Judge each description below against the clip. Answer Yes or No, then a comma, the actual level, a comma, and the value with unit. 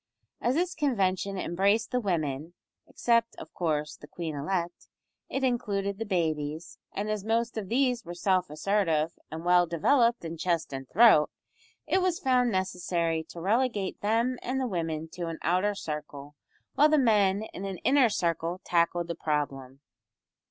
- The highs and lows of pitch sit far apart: Yes, wide, 5.8 semitones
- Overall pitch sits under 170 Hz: No, medium, 185 Hz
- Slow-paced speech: No, average, 160 wpm